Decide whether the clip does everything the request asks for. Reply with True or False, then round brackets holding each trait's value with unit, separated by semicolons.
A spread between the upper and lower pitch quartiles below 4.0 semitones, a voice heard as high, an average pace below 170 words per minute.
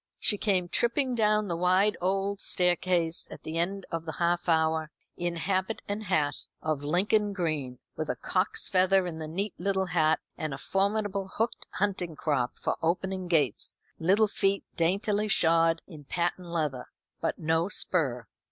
False (3.5 semitones; 180 Hz; 160 wpm)